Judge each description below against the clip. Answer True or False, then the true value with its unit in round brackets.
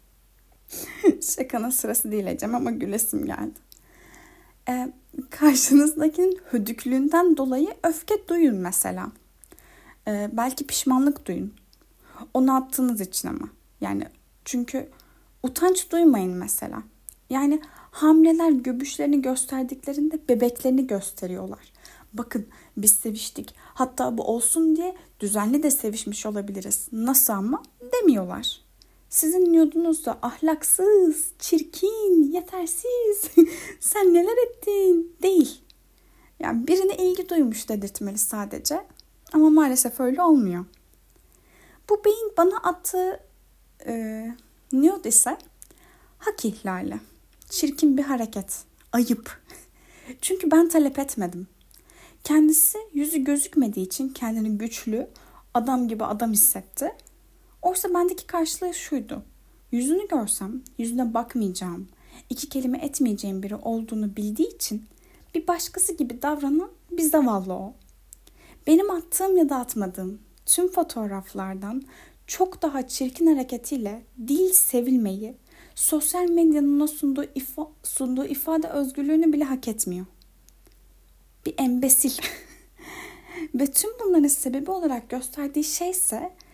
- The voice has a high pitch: True (285 Hz)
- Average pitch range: False (6.2 semitones)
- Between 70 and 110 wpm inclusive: True (105 wpm)